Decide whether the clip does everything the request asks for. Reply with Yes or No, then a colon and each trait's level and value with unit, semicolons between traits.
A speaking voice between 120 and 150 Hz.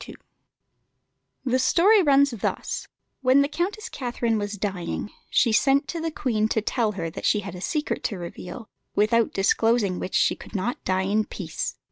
No: high, 225 Hz